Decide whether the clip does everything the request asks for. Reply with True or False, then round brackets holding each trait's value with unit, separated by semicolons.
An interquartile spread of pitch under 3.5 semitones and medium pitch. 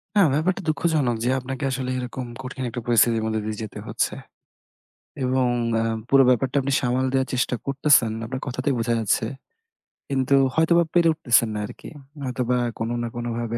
False (2.6 semitones; 130 Hz)